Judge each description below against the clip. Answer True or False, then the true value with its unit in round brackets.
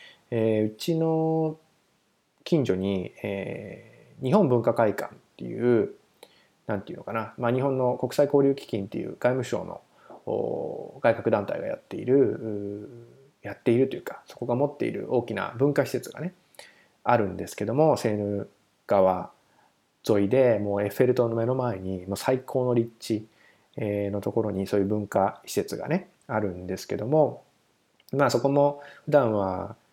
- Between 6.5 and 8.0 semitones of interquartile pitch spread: False (5.4 semitones)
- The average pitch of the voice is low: True (120 Hz)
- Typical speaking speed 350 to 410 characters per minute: False (300 characters per minute)